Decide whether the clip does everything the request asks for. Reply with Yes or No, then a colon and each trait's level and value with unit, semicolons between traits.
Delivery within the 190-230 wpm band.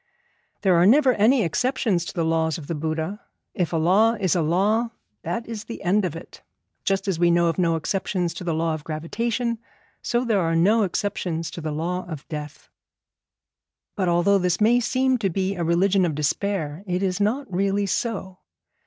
Yes: average, 195 wpm